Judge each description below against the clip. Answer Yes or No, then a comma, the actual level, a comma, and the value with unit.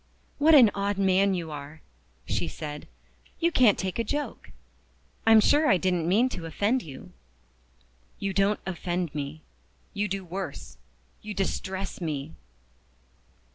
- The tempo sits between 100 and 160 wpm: Yes, slow, 135 wpm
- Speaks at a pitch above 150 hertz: Yes, high, 190 Hz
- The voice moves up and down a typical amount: Yes, average, 4.2 semitones